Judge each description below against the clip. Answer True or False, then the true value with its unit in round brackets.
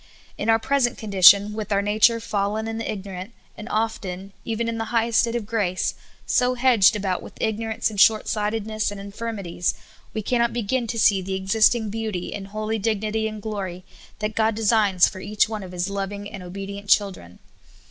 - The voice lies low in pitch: False (210 Hz)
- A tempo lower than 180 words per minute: False (185 wpm)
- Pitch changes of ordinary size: False (2.2 semitones)